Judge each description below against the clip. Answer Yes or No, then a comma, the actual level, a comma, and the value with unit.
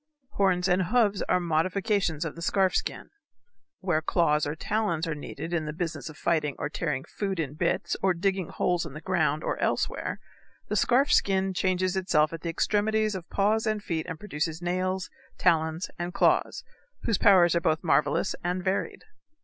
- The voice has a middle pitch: Yes, medium, 180 Hz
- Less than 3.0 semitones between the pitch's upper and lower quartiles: No, average, 3.3 semitones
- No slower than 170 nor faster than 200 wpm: Yes, average, 180 wpm